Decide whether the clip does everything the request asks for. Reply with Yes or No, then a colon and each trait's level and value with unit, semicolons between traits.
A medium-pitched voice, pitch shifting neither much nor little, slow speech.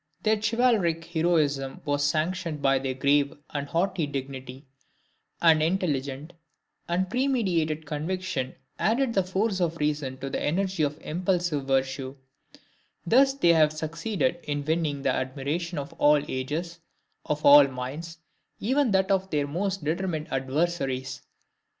Yes: medium, 155 Hz; average, 4.6 semitones; slow, 130 wpm